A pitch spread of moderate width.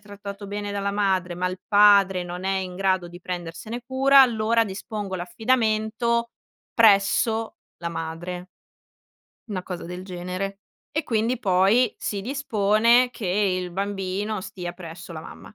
Yes: average, 3.2 semitones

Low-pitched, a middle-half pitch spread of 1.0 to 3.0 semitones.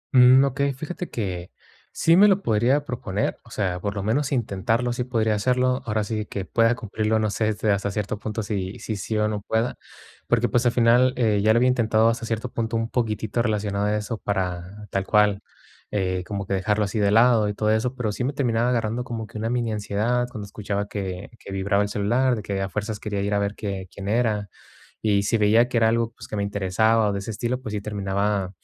Yes: low, 110 Hz; average, 2.7 semitones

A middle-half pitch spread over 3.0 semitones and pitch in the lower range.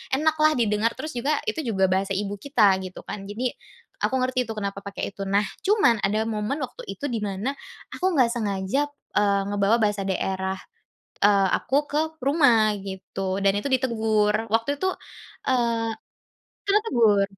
No: average, 4.6 semitones; high, 220 Hz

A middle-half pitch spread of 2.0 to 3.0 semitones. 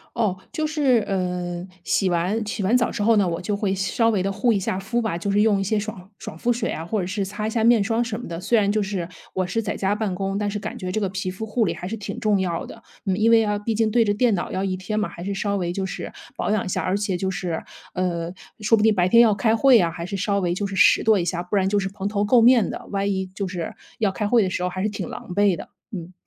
Yes: average, 2.7 semitones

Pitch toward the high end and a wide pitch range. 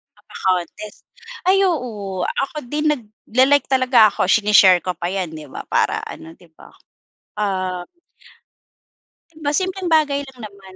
Yes: high, 210 Hz; wide, 7.1 semitones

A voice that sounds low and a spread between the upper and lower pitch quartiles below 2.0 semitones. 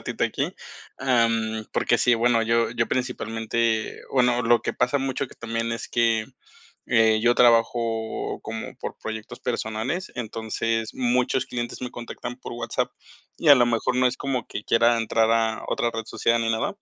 Yes: low, 115 Hz; narrow, 1.5 semitones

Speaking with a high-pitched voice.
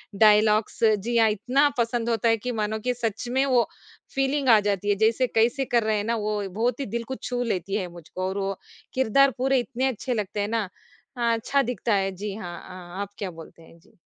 Yes: high, 220 Hz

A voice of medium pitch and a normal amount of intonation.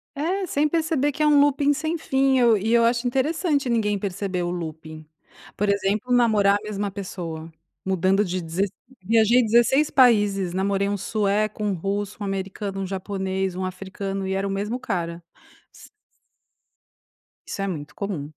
No: high, 200 Hz; average, 4.2 semitones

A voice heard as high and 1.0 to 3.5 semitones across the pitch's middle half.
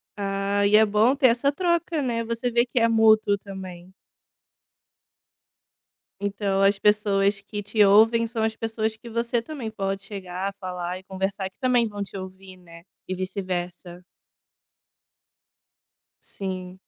Yes: high, 205 Hz; average, 3.1 semitones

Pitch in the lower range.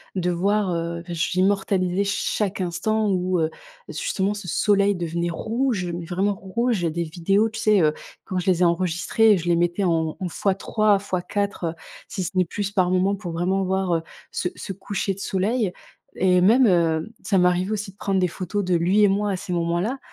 No: medium, 185 Hz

